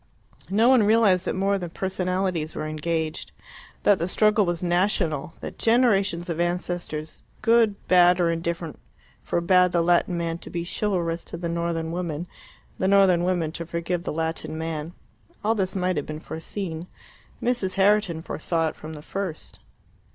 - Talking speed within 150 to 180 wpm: Yes, average, 160 wpm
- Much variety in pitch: No, narrow, 2.6 semitones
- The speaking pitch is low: No, medium, 175 Hz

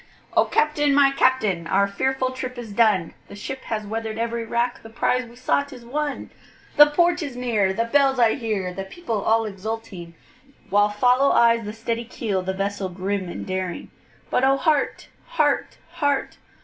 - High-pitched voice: Yes, high, 230 Hz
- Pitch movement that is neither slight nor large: Yes, average, 4.7 semitones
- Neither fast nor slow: Yes, average, 175 wpm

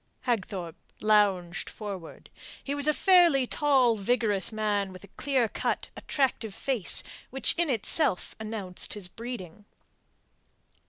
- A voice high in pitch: Yes, high, 220 Hz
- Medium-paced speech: No, slow, 120 wpm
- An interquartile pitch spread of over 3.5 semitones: Yes, wide, 5.4 semitones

